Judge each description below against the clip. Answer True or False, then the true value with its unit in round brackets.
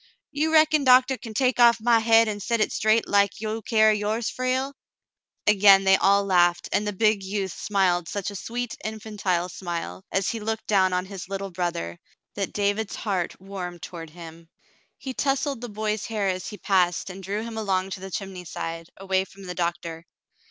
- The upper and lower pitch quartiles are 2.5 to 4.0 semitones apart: True (3.1 semitones)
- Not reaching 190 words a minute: False (195 wpm)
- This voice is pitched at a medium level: False (200 Hz)